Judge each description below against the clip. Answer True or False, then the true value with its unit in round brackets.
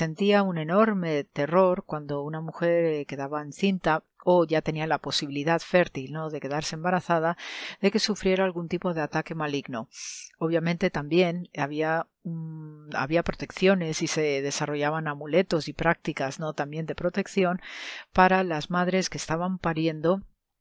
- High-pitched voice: False (165 Hz)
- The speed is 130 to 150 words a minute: True (145 wpm)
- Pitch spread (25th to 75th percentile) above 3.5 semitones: False (3.2 semitones)